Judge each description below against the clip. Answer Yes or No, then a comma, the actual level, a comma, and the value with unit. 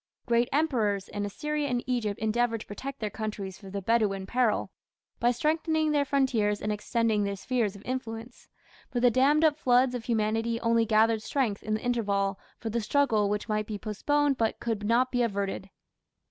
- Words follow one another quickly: No, average, 185 wpm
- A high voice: Yes, high, 230 Hz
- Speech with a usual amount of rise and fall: Yes, average, 3.3 semitones